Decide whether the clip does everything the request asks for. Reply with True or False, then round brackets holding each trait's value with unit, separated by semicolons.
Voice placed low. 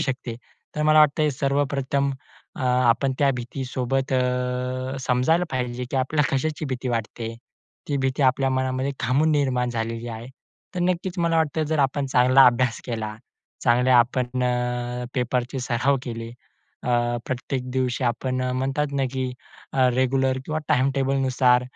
True (130 Hz)